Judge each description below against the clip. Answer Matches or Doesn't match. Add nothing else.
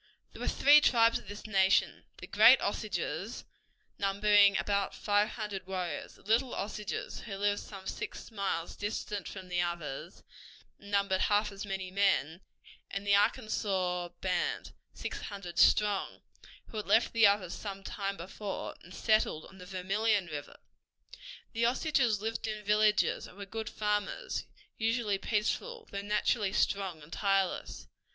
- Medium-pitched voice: Doesn't match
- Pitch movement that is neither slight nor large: Doesn't match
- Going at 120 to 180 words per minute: Matches